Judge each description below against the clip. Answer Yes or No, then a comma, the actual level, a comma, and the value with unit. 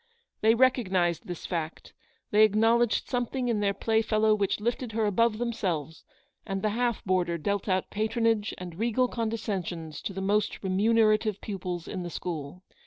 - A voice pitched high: Yes, high, 210 Hz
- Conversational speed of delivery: Yes, average, 160 wpm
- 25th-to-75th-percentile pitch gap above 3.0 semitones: Yes, average, 3.7 semitones